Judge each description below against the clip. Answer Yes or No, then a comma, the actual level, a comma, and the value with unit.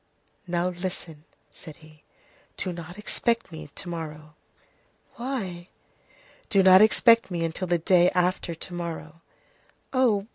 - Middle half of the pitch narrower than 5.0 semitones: Yes, average, 2.7 semitones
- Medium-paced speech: No, slow, 130 wpm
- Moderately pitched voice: Yes, medium, 175 Hz